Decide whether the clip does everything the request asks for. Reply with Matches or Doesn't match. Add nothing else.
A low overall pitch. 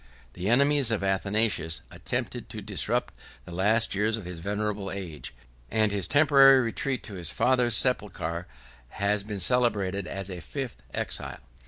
Matches